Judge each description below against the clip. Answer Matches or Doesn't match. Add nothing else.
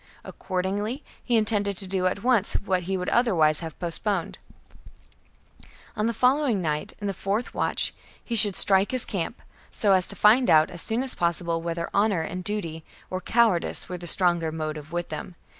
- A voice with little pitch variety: Doesn't match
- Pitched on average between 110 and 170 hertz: Doesn't match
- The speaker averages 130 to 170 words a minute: Doesn't match